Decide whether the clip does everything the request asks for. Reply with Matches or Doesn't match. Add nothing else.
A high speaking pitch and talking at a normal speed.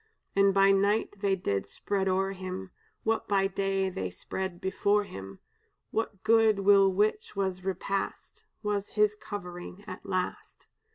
Matches